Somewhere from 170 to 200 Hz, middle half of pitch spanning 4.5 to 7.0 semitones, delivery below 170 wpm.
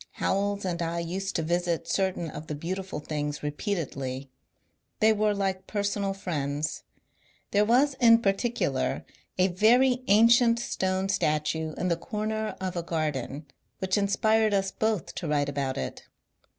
Yes: high, 190 Hz; average, 5.0 semitones; average, 145 wpm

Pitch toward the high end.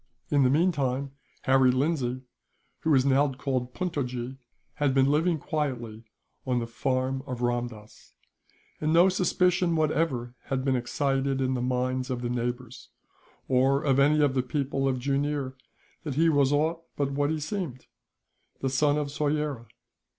No: low, 135 Hz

